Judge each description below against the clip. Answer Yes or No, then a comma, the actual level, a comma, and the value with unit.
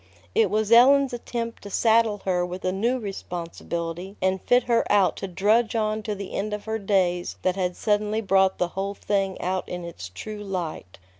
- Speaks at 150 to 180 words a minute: No, average, 195 wpm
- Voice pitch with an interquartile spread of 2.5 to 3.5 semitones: Yes, average, 3.1 semitones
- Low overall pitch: No, high, 200 Hz